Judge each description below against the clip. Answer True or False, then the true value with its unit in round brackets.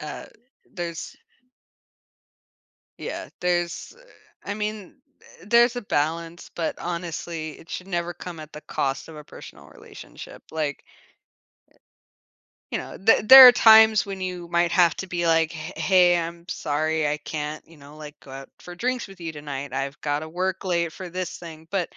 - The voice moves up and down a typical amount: True (3.1 semitones)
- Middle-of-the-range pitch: True (170 Hz)